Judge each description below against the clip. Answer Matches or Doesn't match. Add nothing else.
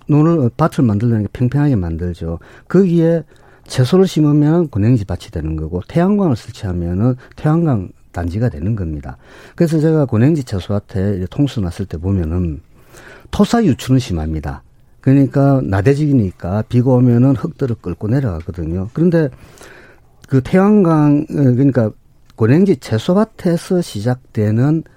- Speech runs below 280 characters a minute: Doesn't match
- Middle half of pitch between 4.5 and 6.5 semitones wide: Doesn't match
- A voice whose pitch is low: Matches